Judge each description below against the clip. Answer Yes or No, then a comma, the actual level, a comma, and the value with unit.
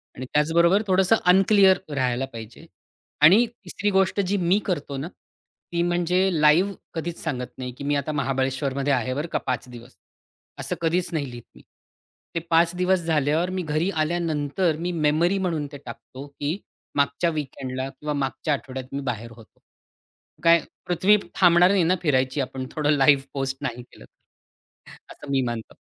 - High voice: No, medium, 150 Hz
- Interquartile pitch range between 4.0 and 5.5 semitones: Yes, average, 4.7 semitones